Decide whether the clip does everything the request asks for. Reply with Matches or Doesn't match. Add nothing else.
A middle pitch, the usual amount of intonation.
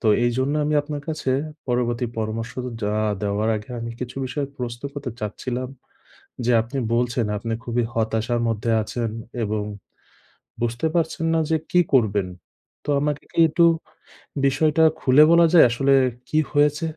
Doesn't match